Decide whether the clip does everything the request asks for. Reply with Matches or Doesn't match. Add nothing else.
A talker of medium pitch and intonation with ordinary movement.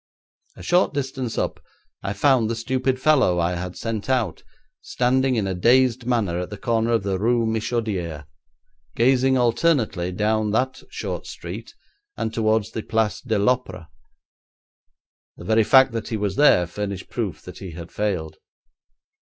Doesn't match